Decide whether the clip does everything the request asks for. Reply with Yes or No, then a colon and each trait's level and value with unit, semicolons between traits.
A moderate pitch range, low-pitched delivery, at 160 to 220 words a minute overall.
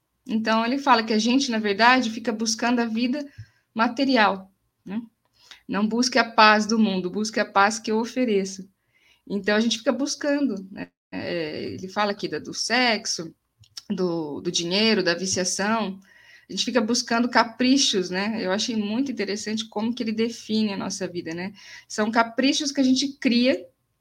No: average, 3.6 semitones; high, 220 Hz; average, 170 wpm